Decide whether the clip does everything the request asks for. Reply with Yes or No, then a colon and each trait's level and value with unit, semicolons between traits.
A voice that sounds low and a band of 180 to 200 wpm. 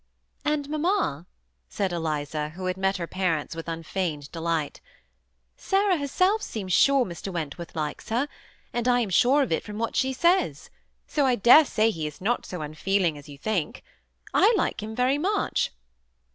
No: high, 195 Hz; average, 185 wpm